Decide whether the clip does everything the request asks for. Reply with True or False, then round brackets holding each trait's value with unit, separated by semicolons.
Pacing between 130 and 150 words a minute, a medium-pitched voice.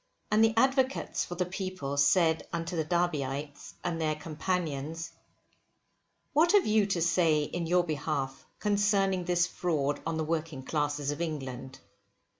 True (145 wpm; 165 Hz)